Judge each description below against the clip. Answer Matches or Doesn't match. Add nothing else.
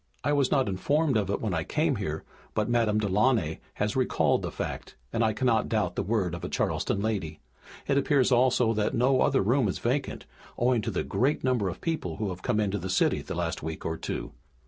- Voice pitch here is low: Matches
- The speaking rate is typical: Doesn't match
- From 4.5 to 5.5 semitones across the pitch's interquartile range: Matches